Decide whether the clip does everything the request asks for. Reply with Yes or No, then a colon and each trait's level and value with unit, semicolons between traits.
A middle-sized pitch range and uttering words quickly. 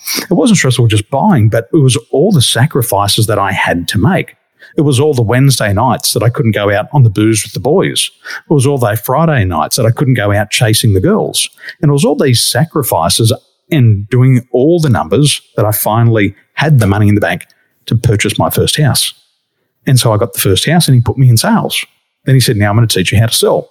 Yes: average, 4.5 semitones; fast, 245 wpm